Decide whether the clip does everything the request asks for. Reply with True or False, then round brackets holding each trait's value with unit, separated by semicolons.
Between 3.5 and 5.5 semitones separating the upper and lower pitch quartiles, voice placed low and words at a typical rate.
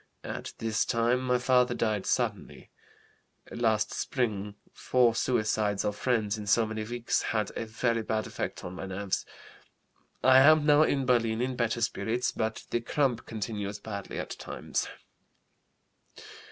False (2.7 semitones; 115 Hz; 145 wpm)